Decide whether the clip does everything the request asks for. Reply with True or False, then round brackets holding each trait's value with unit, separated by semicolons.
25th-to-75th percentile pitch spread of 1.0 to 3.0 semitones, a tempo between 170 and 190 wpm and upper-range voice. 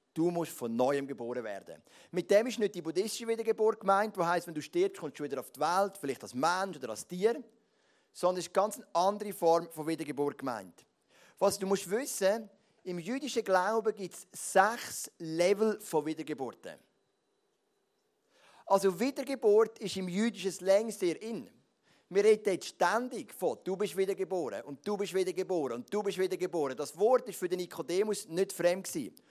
False (4.0 semitones; 180 wpm; 195 Hz)